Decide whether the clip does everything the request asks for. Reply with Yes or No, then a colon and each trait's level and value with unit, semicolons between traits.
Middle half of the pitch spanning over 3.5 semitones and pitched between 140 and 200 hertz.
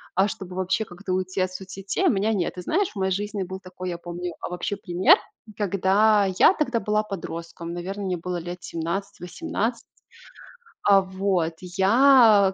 No: narrow, 2.5 semitones; high, 190 Hz